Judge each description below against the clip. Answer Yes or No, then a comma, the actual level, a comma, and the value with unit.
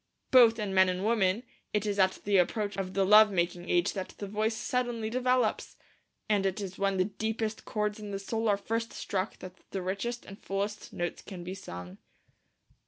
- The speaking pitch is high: Yes, high, 200 Hz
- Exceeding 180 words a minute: Yes, average, 195 wpm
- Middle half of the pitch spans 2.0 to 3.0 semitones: Yes, narrow, 2.6 semitones